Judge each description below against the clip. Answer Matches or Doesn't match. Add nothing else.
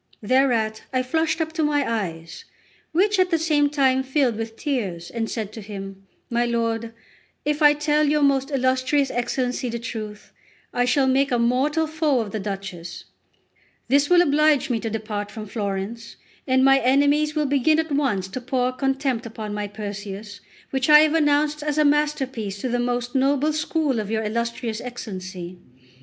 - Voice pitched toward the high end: Matches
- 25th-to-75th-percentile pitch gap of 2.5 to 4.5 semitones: Doesn't match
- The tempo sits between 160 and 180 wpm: Matches